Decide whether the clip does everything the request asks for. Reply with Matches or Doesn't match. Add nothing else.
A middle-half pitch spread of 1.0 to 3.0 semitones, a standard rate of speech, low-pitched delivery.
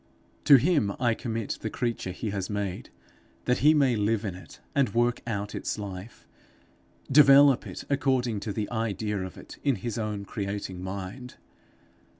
Doesn't match